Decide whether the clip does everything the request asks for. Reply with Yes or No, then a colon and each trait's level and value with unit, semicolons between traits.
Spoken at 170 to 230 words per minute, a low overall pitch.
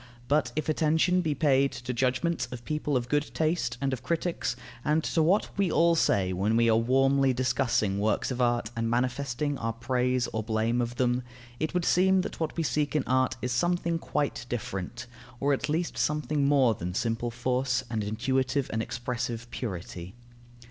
Yes: average, 185 wpm; low, 130 Hz